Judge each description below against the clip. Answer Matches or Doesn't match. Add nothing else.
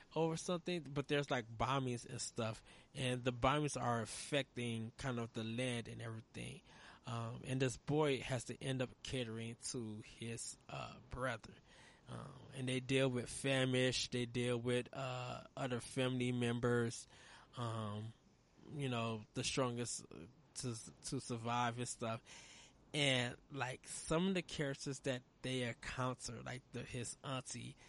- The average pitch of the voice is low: Matches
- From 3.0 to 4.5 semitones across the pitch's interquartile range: Doesn't match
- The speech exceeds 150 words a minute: Doesn't match